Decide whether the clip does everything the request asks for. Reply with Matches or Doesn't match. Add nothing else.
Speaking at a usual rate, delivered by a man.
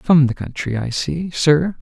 Matches